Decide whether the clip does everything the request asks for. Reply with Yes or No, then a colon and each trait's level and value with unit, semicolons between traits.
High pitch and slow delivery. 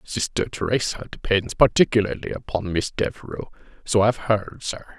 No: low, 105 Hz; slow, 120 wpm